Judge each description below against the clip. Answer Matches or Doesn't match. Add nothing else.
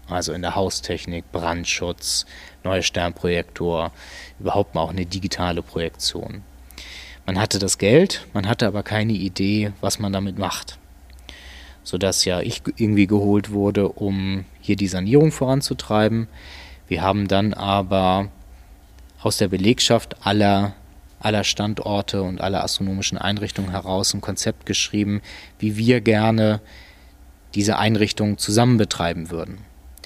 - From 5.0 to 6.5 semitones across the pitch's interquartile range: Doesn't match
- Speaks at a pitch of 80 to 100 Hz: Matches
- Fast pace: Doesn't match